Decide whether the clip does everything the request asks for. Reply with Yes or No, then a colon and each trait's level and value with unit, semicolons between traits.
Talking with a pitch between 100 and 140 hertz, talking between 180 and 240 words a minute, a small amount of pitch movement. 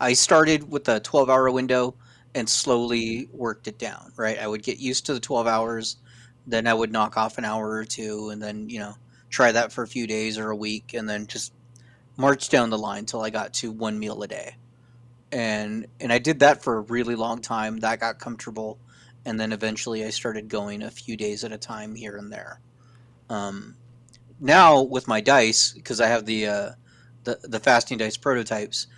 Yes: low, 115 Hz; fast, 205 wpm; narrow, 2.0 semitones